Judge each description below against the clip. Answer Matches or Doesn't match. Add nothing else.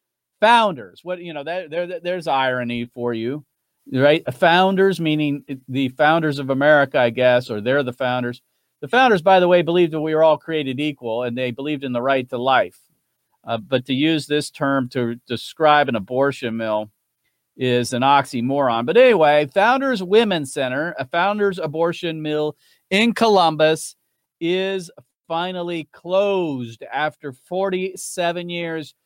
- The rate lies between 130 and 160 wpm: Matches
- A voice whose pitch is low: Doesn't match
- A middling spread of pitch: Matches